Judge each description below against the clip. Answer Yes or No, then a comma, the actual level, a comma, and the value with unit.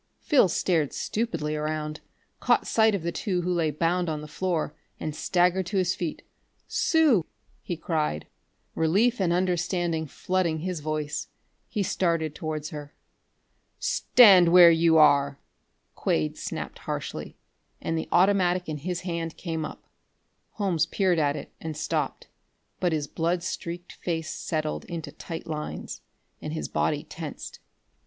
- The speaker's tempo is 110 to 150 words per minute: Yes, average, 145 wpm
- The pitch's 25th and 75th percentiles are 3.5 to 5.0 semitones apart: No, average, 2.8 semitones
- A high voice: No, medium, 170 Hz